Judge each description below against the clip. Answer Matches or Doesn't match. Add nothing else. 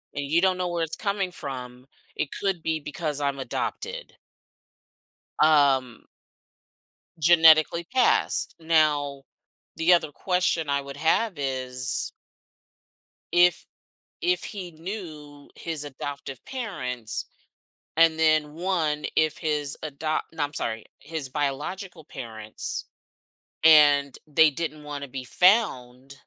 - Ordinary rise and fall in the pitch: Matches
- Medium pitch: Matches